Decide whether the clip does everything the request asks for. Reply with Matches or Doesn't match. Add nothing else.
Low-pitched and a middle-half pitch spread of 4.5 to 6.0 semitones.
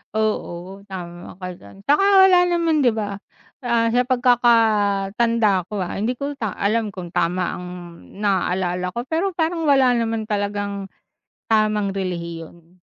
Doesn't match